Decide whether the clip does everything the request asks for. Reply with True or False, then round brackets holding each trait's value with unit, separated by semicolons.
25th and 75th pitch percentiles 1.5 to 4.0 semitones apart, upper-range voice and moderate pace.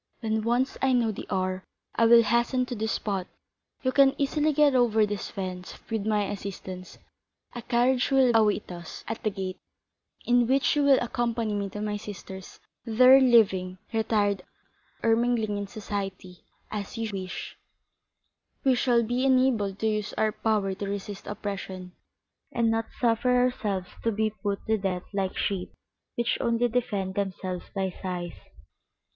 True (3.6 semitones; 215 Hz; 160 wpm)